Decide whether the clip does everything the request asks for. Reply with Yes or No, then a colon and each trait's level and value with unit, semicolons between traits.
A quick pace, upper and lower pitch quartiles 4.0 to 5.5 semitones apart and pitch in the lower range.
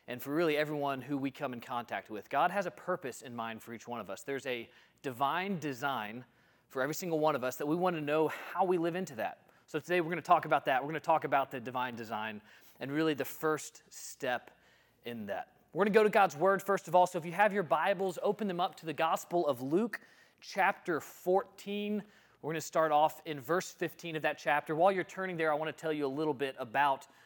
No: fast, 250 wpm; average, 4.6 semitones; medium, 155 Hz